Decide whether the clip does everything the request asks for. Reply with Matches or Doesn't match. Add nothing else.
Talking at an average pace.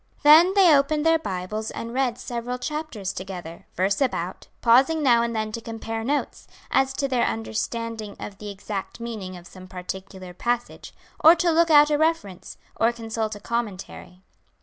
Matches